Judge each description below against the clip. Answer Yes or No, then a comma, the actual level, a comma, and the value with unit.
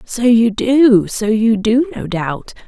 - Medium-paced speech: Yes, average, 180 wpm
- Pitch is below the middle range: No, high, 230 Hz